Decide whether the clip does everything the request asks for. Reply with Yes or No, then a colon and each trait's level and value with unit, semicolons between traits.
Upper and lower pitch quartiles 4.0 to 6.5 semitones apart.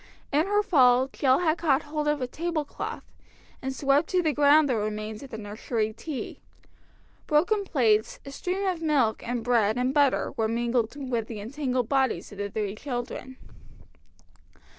Yes: average, 4.8 semitones